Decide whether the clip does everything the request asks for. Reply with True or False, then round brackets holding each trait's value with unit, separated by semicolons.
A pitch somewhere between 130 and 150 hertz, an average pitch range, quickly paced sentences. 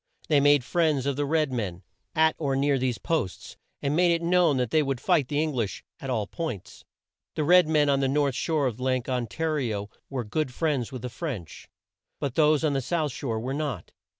True (140 Hz; 3.8 semitones; 225 wpm)